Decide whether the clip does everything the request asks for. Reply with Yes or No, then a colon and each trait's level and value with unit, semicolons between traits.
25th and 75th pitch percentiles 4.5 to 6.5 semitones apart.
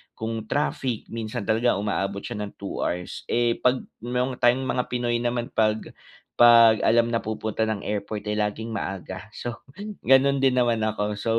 No: narrow, 2.4 semitones